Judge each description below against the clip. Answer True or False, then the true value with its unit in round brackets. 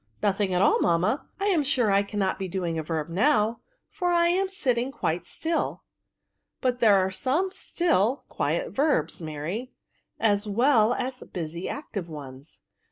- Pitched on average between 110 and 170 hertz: False (210 Hz)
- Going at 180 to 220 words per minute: False (165 wpm)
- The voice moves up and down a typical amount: False (7.7 semitones)